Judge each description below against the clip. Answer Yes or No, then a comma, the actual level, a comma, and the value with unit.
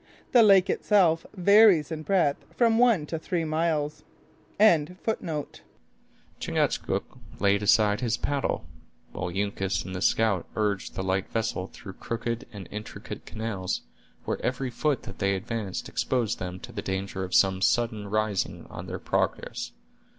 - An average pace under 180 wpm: Yes, average, 145 wpm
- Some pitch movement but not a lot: No, wide, 8.4 semitones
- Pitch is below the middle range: Yes, low, 115 Hz